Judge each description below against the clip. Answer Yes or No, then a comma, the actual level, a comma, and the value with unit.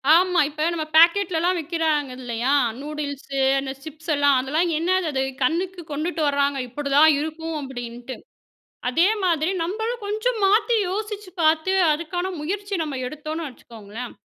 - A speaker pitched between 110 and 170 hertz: No, very high, 315 Hz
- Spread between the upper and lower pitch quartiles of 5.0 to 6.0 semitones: No, average, 4.2 semitones